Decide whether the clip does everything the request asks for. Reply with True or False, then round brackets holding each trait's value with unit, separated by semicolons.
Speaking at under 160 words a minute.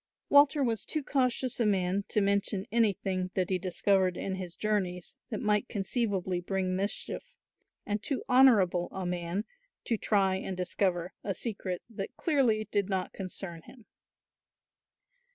True (145 wpm)